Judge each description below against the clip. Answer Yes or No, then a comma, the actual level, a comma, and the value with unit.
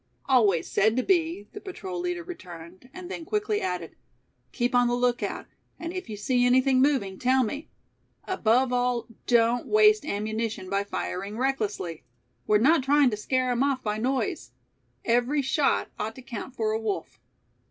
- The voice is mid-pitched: No, high, 245 Hz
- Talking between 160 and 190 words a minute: Yes, average, 165 wpm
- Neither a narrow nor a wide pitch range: Yes, average, 4.8 semitones